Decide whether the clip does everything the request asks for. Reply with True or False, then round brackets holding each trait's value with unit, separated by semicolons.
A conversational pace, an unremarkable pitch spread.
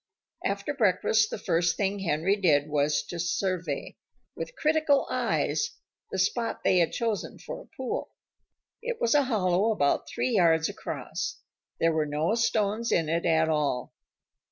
False (155 wpm; 5.8 semitones)